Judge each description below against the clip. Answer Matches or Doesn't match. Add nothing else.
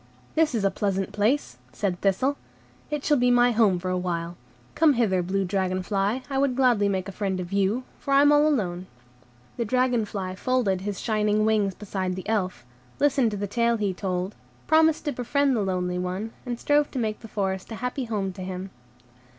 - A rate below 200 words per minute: Doesn't match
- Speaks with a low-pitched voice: Doesn't match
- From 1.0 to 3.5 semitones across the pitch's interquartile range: Doesn't match